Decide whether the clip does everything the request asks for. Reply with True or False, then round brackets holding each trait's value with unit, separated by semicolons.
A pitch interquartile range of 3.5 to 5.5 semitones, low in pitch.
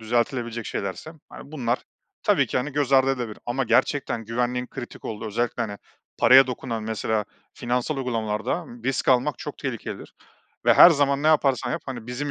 False (2.8 semitones; 125 Hz)